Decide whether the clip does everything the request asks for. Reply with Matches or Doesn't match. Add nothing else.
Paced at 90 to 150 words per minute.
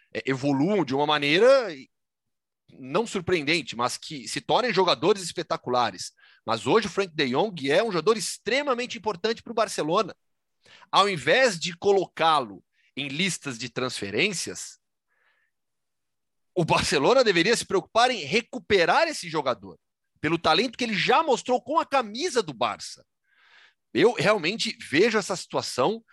Matches